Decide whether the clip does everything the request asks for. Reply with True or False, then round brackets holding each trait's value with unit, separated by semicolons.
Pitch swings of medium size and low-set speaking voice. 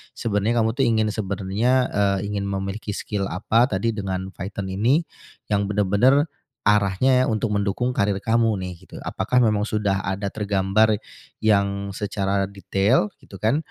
False (2.1 semitones; 105 Hz)